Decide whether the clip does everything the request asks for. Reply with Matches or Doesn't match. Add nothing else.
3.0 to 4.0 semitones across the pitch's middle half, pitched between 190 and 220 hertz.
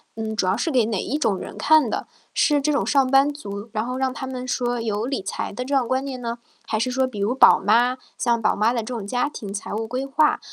Doesn't match